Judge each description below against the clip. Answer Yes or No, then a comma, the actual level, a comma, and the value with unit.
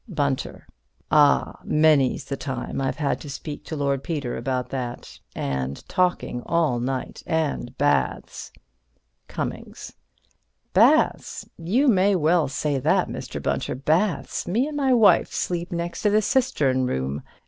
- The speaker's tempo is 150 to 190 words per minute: No, slow, 135 wpm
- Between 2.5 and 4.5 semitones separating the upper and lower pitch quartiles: No, average, 5.2 semitones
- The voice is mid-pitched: Yes, medium, 150 Hz